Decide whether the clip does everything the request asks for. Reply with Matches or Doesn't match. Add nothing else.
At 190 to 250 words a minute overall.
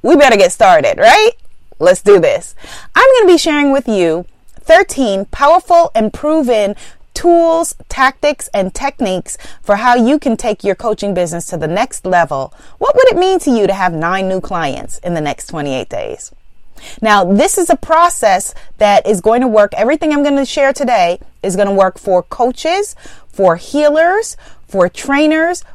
Doesn't match